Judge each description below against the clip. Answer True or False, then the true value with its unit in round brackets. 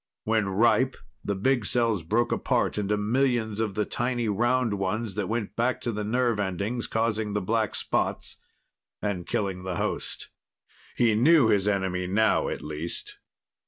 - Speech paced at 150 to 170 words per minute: True (160 wpm)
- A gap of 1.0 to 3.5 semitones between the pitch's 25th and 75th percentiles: True (3.1 semitones)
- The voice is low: True (105 Hz)